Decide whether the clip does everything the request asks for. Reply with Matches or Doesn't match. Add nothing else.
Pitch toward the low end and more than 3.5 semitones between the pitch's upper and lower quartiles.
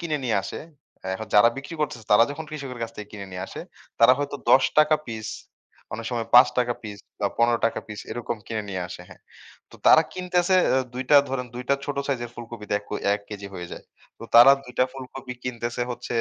Matches